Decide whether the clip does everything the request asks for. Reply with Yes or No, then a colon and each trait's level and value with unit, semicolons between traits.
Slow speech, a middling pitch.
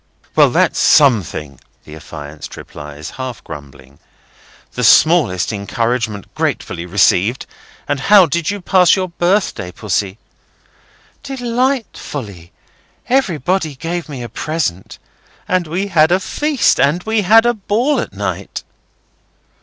Yes: slow, 120 wpm; medium, 145 Hz